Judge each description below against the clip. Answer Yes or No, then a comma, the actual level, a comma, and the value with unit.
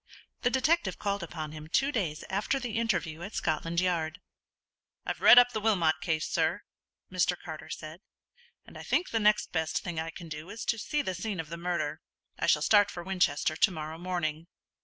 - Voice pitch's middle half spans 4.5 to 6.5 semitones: Yes, average, 4.9 semitones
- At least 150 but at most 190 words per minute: No, average, 200 wpm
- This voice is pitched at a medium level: Yes, medium, 175 Hz